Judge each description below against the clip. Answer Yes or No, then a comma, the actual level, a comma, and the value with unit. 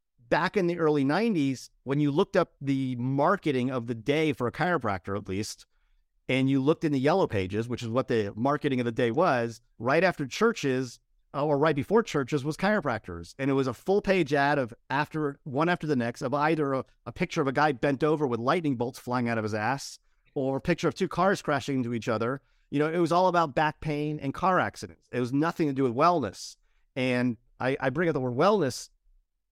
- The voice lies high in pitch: No, medium, 140 Hz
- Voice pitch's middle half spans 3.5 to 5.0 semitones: Yes, average, 4.2 semitones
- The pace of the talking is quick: Yes, fast, 225 wpm